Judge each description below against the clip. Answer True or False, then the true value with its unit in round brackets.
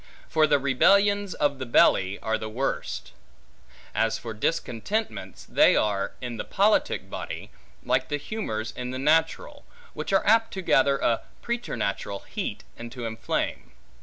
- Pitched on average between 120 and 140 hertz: True (135 Hz)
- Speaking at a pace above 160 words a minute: False (150 wpm)